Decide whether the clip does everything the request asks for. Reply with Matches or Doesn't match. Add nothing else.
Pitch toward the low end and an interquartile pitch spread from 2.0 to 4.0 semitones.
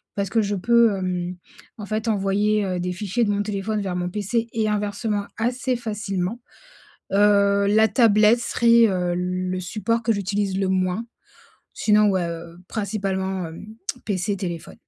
Doesn't match